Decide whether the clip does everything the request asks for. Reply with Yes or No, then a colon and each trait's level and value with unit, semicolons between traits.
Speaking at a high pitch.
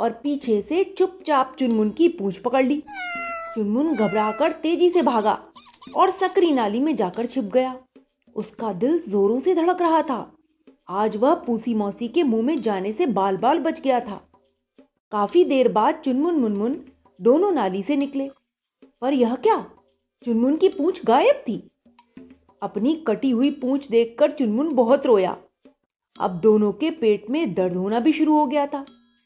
Yes: very high, 260 Hz